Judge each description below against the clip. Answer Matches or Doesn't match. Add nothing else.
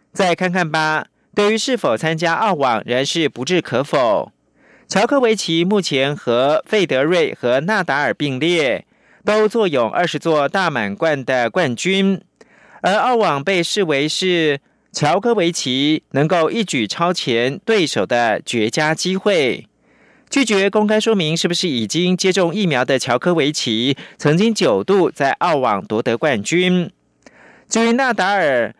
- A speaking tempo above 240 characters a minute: Doesn't match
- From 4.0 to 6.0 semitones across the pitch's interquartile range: Matches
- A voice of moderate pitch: Matches